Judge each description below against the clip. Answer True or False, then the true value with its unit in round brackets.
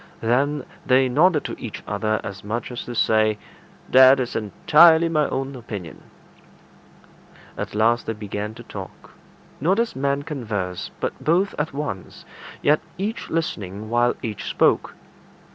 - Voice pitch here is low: True (125 Hz)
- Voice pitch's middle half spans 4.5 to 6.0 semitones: True (5.5 semitones)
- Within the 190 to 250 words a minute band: False (145 wpm)